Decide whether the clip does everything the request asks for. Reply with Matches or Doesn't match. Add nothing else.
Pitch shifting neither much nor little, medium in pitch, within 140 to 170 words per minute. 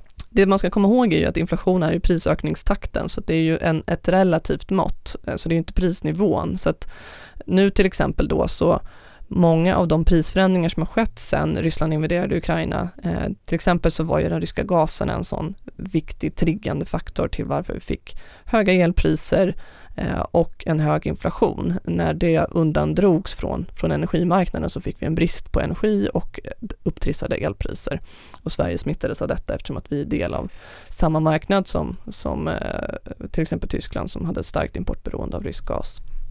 Doesn't match